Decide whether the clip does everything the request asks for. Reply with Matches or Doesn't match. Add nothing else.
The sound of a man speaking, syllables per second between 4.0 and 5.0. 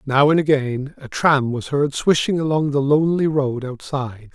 Matches